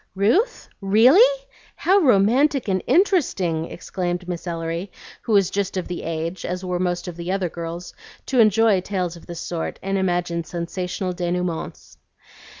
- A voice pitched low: No, medium, 185 Hz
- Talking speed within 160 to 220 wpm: No, average, 150 wpm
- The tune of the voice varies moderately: Yes, average, 3.3 semitones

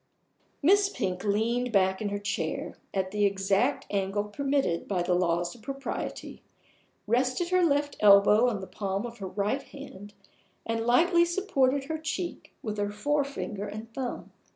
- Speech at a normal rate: Yes, average, 155 wpm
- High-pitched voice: Yes, high, 220 Hz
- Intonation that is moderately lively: No, wide, 5.8 semitones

